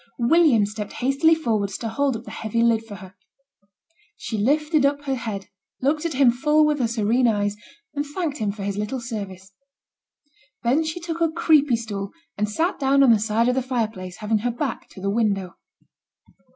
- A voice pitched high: Yes, high, 235 Hz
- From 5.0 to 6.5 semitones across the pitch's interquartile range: Yes, wide, 5.4 semitones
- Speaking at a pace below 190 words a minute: No, average, 195 wpm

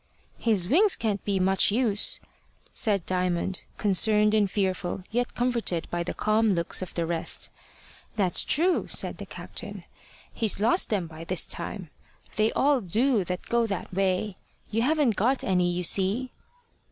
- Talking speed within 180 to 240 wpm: No, average, 155 wpm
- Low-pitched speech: No, high, 205 Hz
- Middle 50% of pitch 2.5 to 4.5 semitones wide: Yes, average, 3.9 semitones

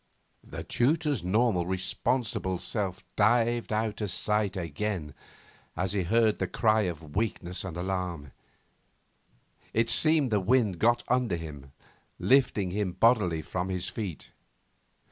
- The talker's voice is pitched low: Yes, low, 100 Hz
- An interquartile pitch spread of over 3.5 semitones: Yes, average, 4.3 semitones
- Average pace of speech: No, slow, 130 wpm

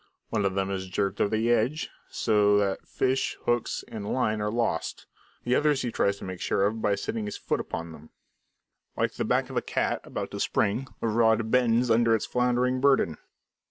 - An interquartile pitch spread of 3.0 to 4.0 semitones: Yes, average, 3.3 semitones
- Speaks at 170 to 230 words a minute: Yes, average, 200 wpm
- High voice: No, low, 110 Hz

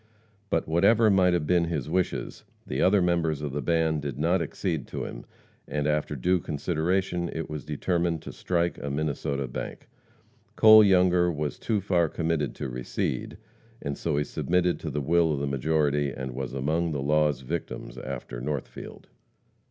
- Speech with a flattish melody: No, average, 3.5 semitones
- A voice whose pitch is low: Yes, very low, 80 Hz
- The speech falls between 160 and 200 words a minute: Yes, average, 170 wpm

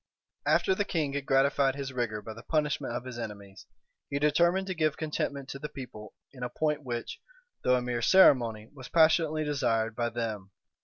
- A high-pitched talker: No, low, 135 Hz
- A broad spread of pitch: No, average, 4.4 semitones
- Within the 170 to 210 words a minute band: Yes, average, 190 wpm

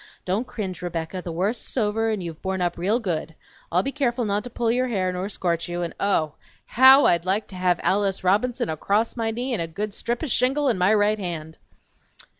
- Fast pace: Yes, fast, 220 wpm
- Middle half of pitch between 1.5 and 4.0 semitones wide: No, average, 4.6 semitones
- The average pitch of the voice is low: No, high, 200 Hz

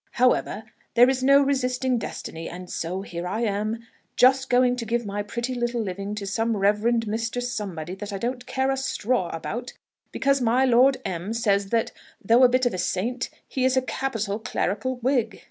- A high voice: Yes, high, 235 Hz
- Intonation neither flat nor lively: Yes, average, 3.9 semitones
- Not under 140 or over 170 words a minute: No, average, 190 wpm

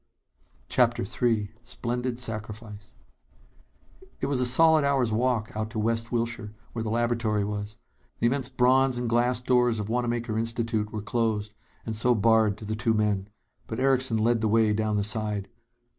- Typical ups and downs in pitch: No, narrow, 2.2 semitones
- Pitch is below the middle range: Yes, low, 115 Hz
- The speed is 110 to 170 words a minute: Yes, average, 165 wpm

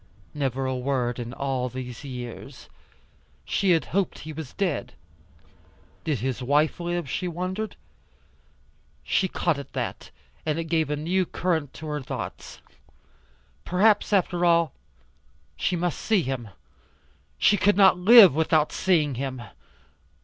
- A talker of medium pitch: Yes, medium, 160 Hz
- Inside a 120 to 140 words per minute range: Yes, slow, 135 wpm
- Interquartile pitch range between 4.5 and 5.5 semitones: Yes, average, 5.1 semitones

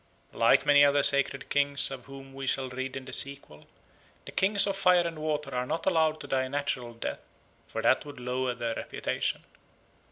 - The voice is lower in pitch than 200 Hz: Yes, medium, 140 Hz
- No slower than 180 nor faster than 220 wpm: Yes, average, 195 wpm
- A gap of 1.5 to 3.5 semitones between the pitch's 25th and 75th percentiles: Yes, narrow, 2.6 semitones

